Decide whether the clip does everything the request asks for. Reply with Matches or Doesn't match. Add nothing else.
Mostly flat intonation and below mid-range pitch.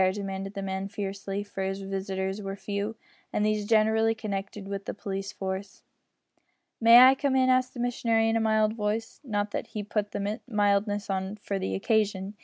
Doesn't match